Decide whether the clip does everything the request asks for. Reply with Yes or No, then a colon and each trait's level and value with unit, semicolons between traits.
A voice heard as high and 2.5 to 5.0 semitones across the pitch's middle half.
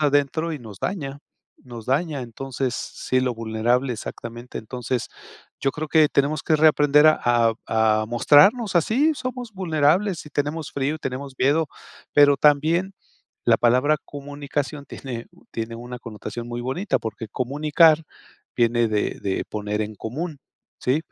No: medium, 140 Hz; average, 4.4 semitones